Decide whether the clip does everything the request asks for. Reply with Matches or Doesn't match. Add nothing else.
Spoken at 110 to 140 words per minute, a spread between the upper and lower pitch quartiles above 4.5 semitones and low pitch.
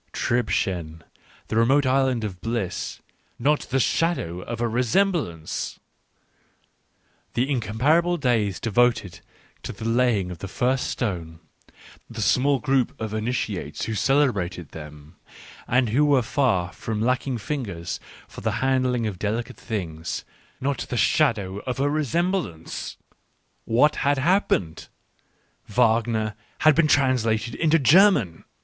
Matches